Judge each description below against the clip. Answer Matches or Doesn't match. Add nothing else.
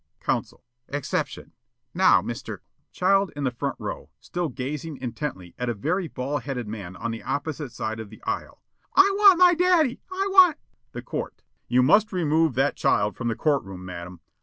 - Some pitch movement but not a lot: Doesn't match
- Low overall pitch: Doesn't match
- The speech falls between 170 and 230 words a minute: Matches